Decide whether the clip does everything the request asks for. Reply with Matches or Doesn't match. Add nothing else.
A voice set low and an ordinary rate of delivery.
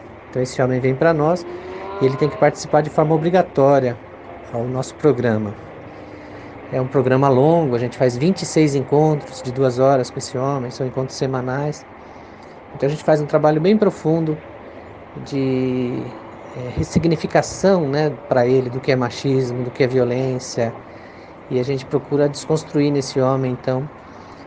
Matches